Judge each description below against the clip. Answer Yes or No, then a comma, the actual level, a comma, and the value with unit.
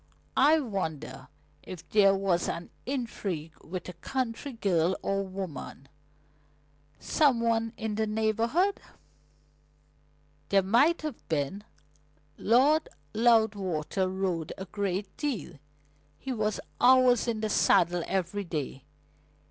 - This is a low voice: No, high, 205 Hz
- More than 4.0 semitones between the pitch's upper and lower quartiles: Yes, average, 4.6 semitones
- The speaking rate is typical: No, slow, 110 wpm